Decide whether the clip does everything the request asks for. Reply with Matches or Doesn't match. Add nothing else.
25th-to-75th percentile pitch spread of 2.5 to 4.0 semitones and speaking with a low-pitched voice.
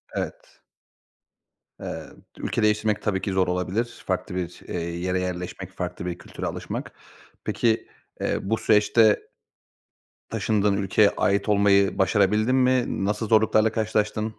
Matches